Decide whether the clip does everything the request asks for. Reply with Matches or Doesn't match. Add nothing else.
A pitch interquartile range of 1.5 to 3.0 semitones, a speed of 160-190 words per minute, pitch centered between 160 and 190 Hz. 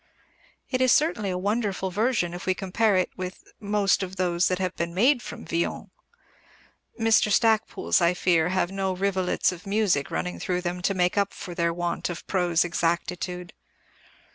Matches